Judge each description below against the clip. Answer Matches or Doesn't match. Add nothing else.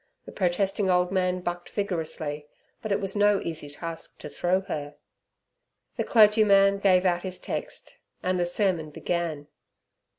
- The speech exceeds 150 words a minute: Doesn't match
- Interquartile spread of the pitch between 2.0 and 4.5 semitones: Matches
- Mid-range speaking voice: Matches